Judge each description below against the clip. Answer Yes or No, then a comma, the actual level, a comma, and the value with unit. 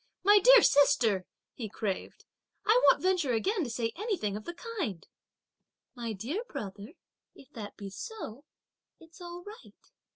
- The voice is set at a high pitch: Yes, very high, 280 Hz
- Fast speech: No, average, 150 wpm